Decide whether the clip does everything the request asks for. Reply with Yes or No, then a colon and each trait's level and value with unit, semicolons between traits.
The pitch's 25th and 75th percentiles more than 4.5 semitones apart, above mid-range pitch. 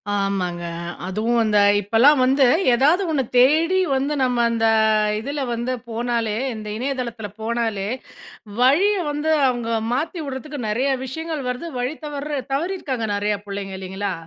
Yes: average, 4.9 semitones; very high, 250 Hz